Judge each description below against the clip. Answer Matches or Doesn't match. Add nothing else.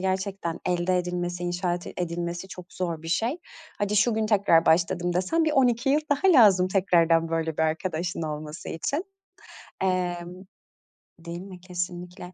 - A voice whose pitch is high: Doesn't match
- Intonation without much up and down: Matches